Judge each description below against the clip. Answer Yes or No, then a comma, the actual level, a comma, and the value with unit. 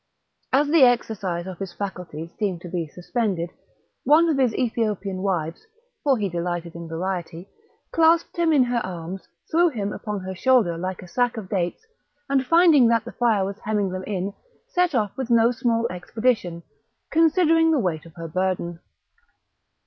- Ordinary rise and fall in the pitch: No, wide, 6.2 semitones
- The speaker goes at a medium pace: Yes, average, 170 wpm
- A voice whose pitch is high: Yes, high, 205 Hz